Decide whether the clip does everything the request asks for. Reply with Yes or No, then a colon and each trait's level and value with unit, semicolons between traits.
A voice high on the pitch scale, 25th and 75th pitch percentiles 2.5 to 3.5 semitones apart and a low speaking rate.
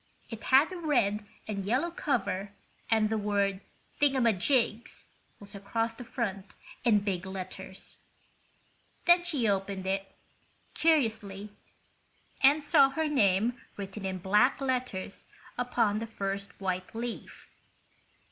No: high, 215 Hz; average, 4.5 semitones; slow, 120 wpm